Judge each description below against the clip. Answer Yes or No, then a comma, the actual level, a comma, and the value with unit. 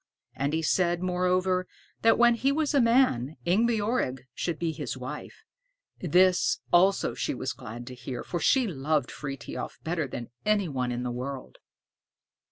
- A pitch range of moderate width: No, wide, 6.8 semitones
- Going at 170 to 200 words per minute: No, average, 160 wpm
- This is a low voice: No, medium, 170 Hz